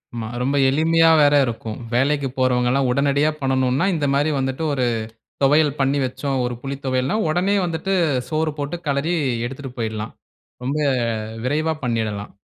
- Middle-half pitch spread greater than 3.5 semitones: No, average, 3.1 semitones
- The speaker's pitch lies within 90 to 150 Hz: Yes, medium, 140 Hz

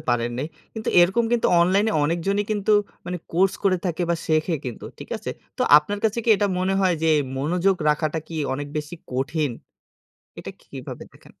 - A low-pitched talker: No, medium, 175 Hz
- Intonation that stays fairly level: No, average, 4.6 semitones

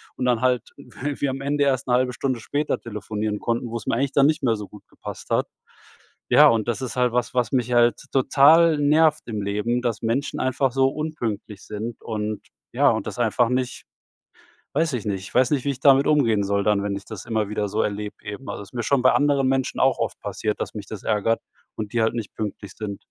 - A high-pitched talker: No, low, 120 Hz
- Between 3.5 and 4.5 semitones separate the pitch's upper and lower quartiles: Yes, average, 4.1 semitones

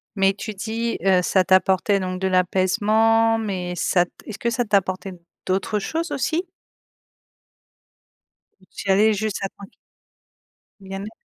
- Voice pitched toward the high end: Yes, high, 195 Hz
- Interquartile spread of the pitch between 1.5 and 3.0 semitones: Yes, average, 2.7 semitones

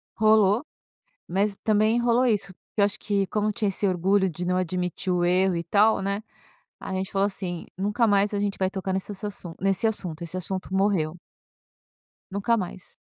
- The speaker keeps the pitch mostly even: Yes, narrow, 2.1 semitones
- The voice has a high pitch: Yes, high, 195 Hz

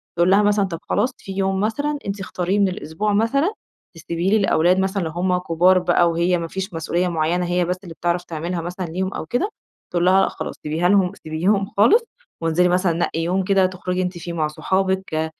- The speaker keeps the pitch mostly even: Yes, narrow, 2.3 semitones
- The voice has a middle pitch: Yes, medium, 180 Hz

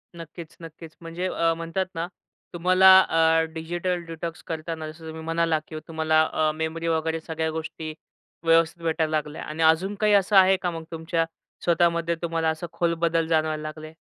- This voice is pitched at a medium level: Yes, medium, 165 Hz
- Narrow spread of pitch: Yes, narrow, 1.1 semitones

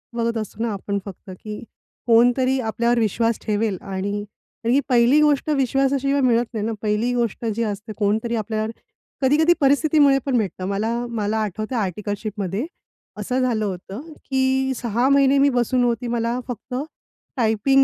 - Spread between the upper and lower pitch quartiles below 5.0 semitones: Yes, average, 3.7 semitones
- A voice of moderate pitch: No, high, 235 Hz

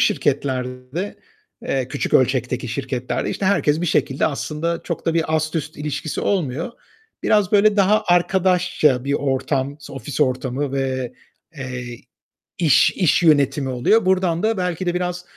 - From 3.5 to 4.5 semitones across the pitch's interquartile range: No, average, 5.3 semitones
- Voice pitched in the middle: Yes, medium, 150 Hz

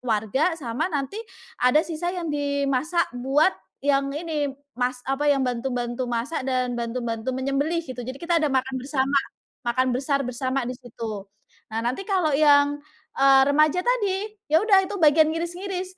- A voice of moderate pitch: No, very high, 275 Hz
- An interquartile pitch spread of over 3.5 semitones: Yes, average, 4.0 semitones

